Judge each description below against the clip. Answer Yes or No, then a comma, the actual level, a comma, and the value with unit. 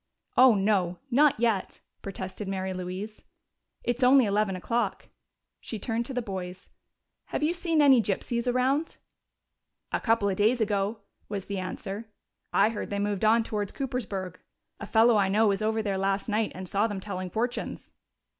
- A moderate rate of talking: Yes, average, 165 wpm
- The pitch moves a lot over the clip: No, average, 3.4 semitones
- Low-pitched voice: No, high, 210 Hz